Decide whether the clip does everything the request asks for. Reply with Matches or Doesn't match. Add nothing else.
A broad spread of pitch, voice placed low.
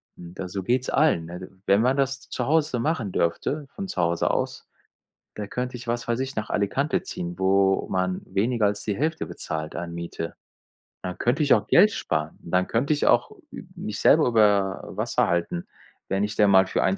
Matches